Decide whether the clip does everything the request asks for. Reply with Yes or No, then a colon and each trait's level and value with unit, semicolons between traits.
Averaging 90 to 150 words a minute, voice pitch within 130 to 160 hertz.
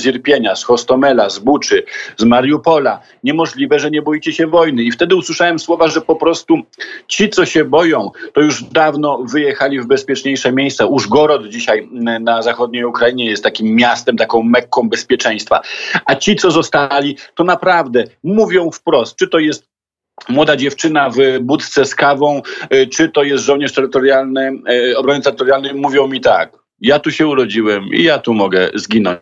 No: fast, 160 wpm; medium, 140 Hz